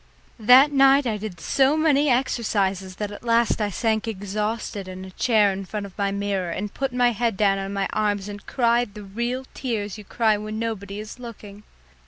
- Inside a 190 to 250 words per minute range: Yes, average, 200 wpm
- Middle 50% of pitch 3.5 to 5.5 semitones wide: No, average, 3.1 semitones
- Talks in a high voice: Yes, high, 215 Hz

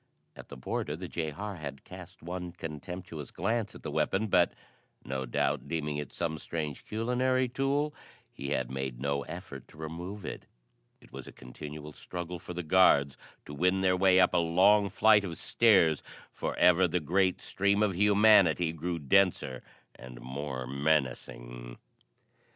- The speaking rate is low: No, average, 160 wpm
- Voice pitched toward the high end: No, very low, 85 Hz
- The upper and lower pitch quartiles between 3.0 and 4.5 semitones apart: No, average, 4.9 semitones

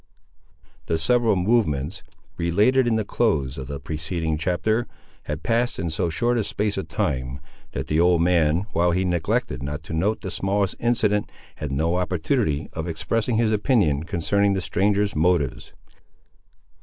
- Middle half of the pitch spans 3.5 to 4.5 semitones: No, average, 5.1 semitones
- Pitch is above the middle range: No, very low, 90 Hz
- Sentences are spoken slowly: No, average, 155 wpm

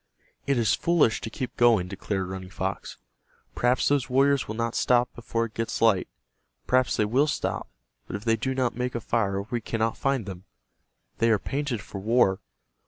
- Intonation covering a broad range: No, average, 3.4 semitones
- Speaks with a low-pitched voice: Yes, low, 115 Hz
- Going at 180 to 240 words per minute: Yes, average, 185 wpm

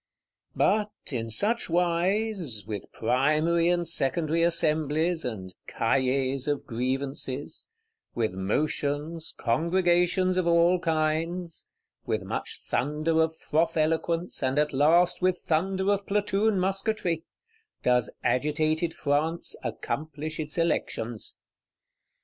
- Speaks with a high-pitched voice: No, medium, 160 Hz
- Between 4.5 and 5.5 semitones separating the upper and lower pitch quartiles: No, average, 3.8 semitones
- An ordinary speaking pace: No, slow, 105 wpm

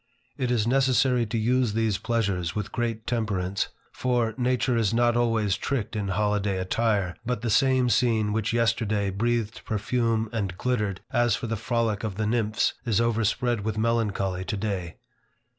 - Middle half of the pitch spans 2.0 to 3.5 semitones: Yes, narrow, 2.5 semitones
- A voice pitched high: No, low, 110 Hz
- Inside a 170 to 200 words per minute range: No, average, 160 wpm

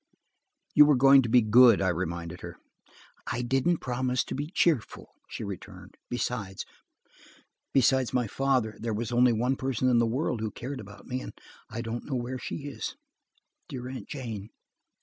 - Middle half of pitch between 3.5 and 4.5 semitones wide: No, average, 3.1 semitones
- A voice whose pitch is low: Yes, low, 125 Hz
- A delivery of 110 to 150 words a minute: No, average, 170 wpm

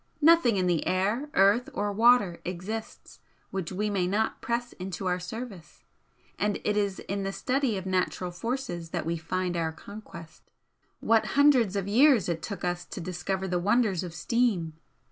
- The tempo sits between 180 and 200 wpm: No, average, 170 wpm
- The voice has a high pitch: Yes, high, 195 Hz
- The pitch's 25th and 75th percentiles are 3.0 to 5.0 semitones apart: Yes, average, 4.1 semitones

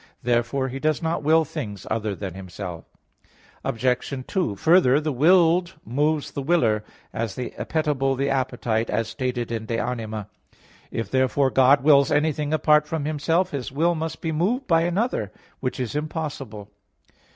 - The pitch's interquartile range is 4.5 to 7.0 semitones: Yes, average, 5.2 semitones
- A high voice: No, low, 135 Hz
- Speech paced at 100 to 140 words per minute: No, average, 160 wpm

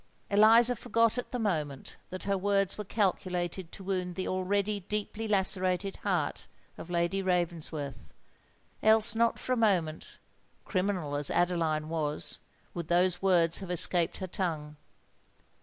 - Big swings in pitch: No, average, 3.2 semitones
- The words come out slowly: Yes, slow, 125 wpm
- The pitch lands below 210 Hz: Yes, medium, 185 Hz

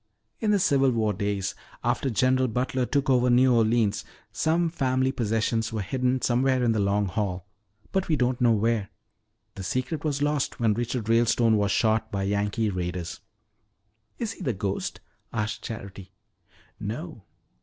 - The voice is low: Yes, low, 115 Hz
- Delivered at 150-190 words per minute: Yes, average, 155 wpm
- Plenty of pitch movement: No, average, 4.0 semitones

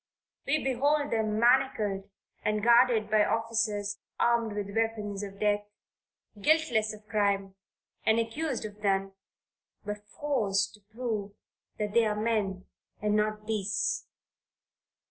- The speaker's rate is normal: No, slow, 125 wpm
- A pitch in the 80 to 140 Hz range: No, high, 215 Hz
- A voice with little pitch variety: Yes, narrow, 2.1 semitones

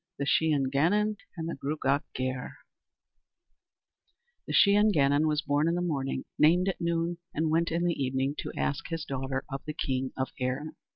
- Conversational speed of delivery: Yes, average, 185 wpm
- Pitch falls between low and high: Yes, medium, 150 Hz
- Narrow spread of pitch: No, average, 3.7 semitones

